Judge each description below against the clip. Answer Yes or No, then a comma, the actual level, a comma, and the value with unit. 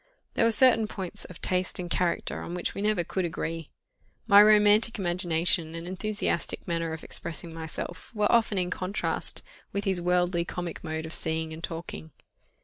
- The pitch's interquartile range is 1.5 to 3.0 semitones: No, average, 3.5 semitones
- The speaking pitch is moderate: Yes, medium, 175 Hz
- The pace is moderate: Yes, average, 170 wpm